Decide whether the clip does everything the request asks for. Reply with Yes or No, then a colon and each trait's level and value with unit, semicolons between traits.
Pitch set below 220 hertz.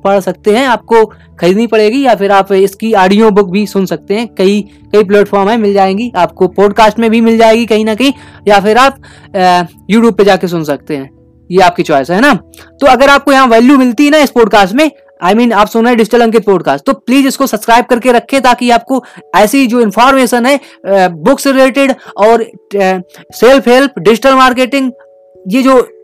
No: high, 225 Hz